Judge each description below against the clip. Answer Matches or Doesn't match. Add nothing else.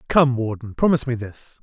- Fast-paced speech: Doesn't match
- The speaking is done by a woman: Doesn't match